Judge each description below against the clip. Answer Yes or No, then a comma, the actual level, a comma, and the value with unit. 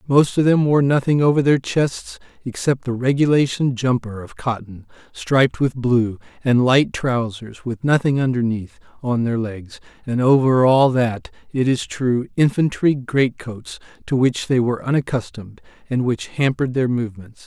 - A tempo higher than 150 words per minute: Yes, average, 160 wpm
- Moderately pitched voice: No, low, 125 Hz